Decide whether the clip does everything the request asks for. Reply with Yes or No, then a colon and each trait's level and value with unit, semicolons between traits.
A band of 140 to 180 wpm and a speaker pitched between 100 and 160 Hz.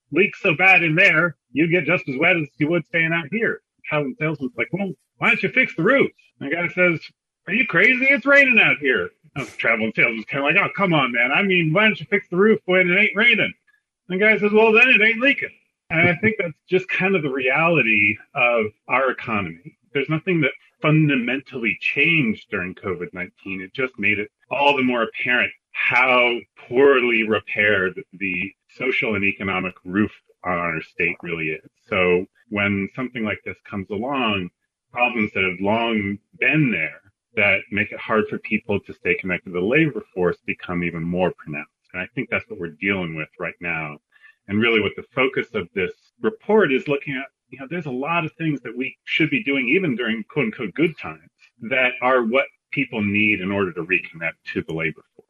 No: fast, 205 wpm; medium, 140 Hz